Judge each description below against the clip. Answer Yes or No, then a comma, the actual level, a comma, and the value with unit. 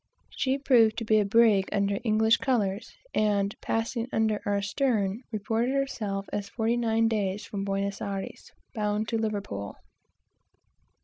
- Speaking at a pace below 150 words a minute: Yes, average, 140 wpm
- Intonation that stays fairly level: Yes, narrow, 2.3 semitones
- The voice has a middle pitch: No, high, 215 Hz